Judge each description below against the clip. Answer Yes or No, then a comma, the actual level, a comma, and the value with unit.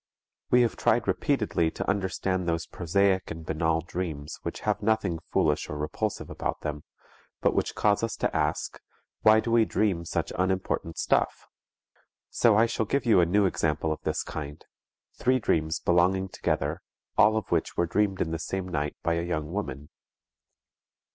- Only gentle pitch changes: No, average, 4.1 semitones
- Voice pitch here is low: Yes, very low, 90 Hz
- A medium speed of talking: Yes, average, 170 wpm